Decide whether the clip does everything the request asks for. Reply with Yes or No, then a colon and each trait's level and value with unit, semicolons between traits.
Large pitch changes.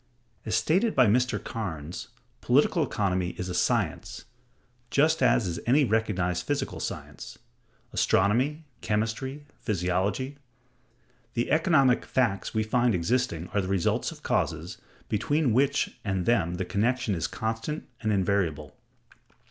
Yes: wide, 5.7 semitones